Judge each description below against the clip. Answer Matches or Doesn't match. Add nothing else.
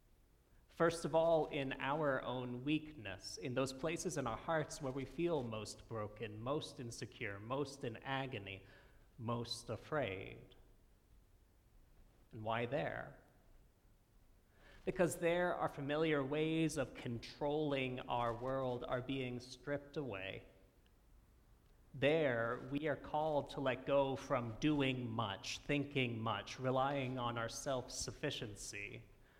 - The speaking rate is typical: Doesn't match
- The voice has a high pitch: Doesn't match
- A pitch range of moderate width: Matches